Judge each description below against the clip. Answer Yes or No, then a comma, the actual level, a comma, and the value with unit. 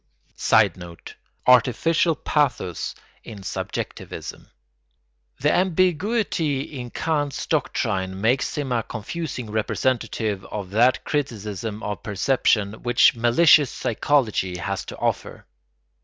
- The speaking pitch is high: No, low, 120 Hz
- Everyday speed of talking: No, slow, 95 wpm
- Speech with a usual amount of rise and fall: No, wide, 5.9 semitones